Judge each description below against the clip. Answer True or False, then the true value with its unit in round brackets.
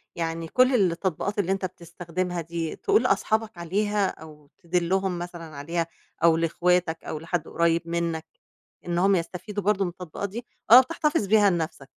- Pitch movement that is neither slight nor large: True (3.0 semitones)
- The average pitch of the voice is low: False (175 Hz)